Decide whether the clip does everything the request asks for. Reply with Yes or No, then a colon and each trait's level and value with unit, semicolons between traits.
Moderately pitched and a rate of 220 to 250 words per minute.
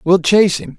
Yes: medium, 175 Hz; fast, 230 wpm